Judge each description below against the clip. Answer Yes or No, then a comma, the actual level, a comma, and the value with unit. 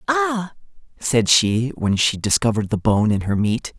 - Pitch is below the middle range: Yes, low, 120 Hz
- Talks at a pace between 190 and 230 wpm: No, average, 175 wpm